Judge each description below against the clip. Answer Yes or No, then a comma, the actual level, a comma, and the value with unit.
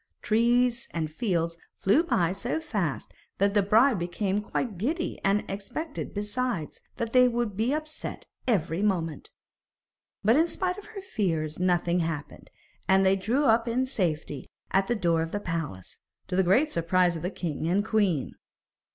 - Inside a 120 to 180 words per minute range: Yes, average, 165 wpm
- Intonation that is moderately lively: No, wide, 5.9 semitones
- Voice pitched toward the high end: Yes, high, 200 Hz